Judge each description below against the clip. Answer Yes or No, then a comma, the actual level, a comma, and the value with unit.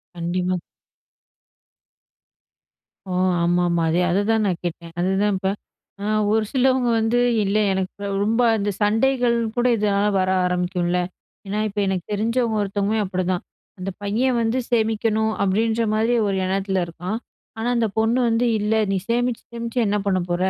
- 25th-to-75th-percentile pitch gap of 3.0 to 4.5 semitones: Yes, average, 3.4 semitones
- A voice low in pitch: No, high, 205 Hz